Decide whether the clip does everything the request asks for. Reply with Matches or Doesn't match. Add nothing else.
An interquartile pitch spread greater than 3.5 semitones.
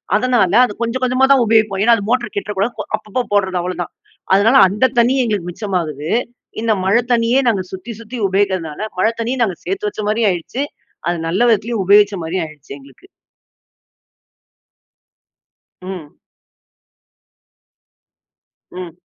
Matches